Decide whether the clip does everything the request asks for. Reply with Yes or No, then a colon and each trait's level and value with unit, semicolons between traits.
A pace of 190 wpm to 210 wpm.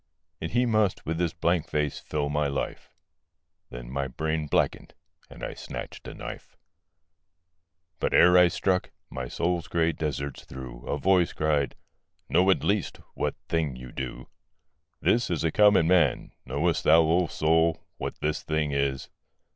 No: average, 155 wpm